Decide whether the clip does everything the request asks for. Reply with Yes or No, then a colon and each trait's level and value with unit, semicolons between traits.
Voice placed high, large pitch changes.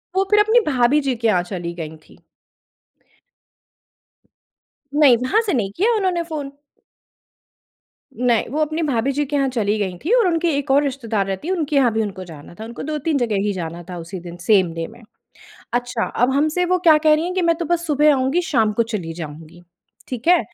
Yes: very high, 260 Hz; wide, 7.7 semitones